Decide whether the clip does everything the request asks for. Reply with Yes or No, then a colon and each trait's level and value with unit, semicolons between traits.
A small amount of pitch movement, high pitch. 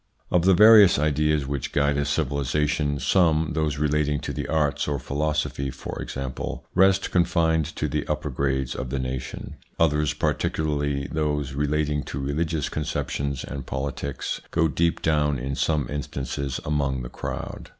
No: narrow, 1.9 semitones; very low, 75 Hz